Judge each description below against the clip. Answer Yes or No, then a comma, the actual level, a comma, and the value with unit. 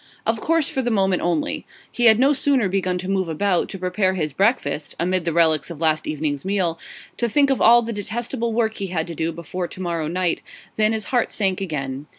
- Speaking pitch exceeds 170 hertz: Yes, medium, 185 Hz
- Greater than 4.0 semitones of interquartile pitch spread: Yes, average, 5.1 semitones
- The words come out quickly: Yes, fast, 220 wpm